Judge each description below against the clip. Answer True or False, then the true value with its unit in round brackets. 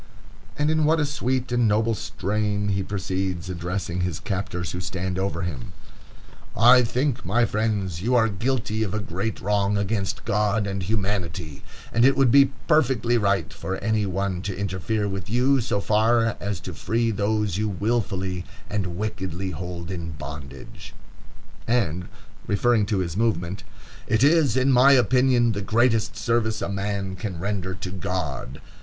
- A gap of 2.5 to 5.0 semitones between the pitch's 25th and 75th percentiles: True (3.7 semitones)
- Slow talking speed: False (160 wpm)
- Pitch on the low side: True (100 Hz)